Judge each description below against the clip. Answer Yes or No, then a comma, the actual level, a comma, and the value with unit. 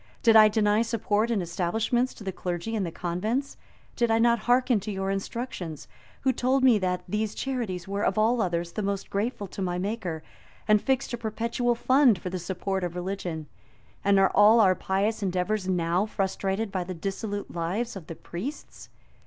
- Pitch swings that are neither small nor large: Yes, average, 3.8 semitones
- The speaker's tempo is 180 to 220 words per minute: Yes, average, 185 wpm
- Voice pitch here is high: Yes, high, 200 Hz